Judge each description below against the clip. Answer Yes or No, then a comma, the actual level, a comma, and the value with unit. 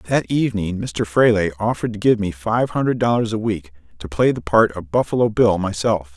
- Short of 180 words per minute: No, fast, 205 wpm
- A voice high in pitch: No, low, 105 Hz